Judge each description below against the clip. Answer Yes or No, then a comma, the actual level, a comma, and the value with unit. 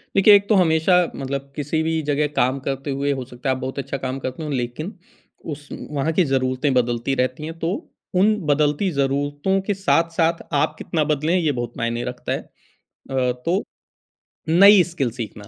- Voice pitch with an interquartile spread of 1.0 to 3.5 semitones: No, average, 4.0 semitones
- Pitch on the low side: No, medium, 145 Hz